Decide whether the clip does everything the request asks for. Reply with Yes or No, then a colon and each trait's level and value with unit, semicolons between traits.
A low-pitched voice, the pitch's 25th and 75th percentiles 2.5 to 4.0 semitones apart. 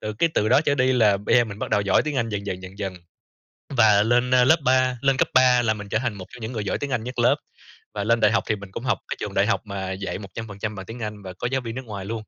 Yes: low, 110 Hz; average, 3.7 semitones